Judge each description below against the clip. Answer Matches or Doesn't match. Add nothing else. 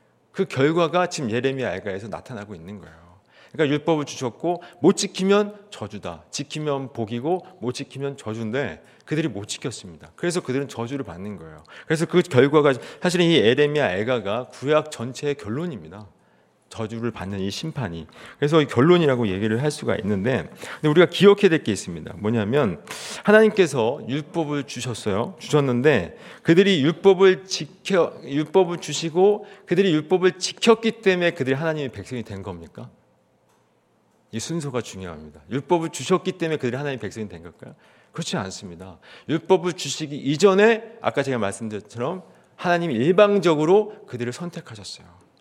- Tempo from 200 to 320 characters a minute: Doesn't match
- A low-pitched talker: Doesn't match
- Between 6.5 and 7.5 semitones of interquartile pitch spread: Matches